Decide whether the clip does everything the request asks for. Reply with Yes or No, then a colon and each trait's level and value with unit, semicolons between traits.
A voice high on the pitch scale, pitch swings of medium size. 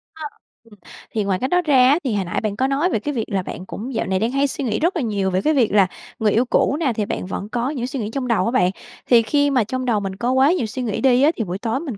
Yes: high, 235 Hz; average, 4.7 semitones